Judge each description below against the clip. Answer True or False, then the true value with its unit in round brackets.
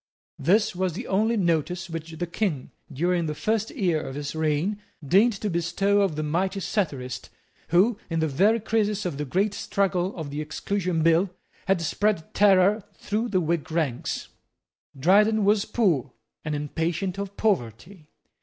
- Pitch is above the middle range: False (180 Hz)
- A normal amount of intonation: True (4.2 semitones)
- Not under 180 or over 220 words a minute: False (160 wpm)